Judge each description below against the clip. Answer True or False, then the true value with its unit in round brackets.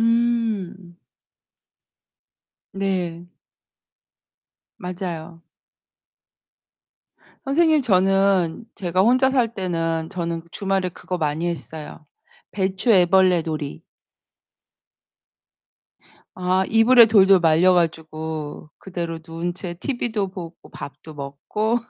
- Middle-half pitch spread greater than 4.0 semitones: False (3.3 semitones)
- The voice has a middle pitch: True (180 Hz)